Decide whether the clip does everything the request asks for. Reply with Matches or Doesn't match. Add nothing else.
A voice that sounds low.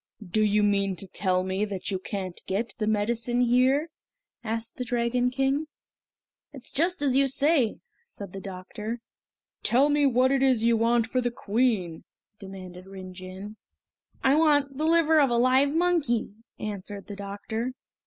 Doesn't match